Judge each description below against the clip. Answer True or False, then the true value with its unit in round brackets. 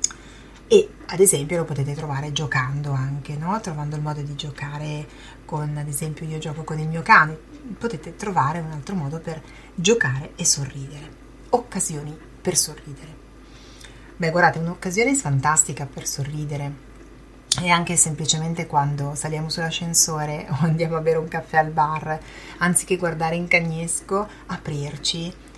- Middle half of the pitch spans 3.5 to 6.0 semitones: False (2.4 semitones)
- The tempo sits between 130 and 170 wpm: True (140 wpm)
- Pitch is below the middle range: False (155 Hz)